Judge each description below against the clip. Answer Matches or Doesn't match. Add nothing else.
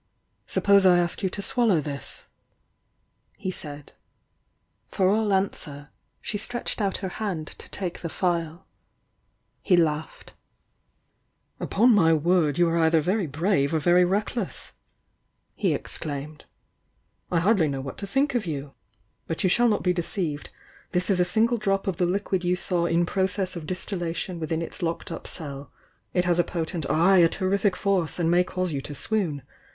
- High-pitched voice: Doesn't match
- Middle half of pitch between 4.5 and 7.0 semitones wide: Doesn't match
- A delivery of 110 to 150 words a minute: Doesn't match